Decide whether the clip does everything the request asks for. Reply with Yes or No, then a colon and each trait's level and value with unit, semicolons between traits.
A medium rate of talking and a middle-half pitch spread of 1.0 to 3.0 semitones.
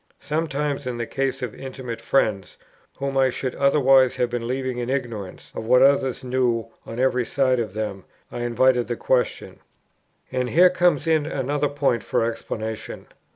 Yes: average, 165 wpm; narrow, 2.5 semitones